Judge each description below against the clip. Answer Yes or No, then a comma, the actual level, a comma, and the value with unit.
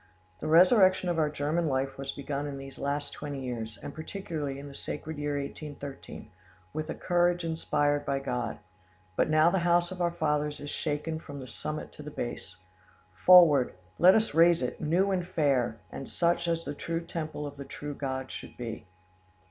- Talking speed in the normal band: Yes, average, 190 wpm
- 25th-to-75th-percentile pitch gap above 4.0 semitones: No, average, 3.4 semitones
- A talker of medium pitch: Yes, medium, 150 Hz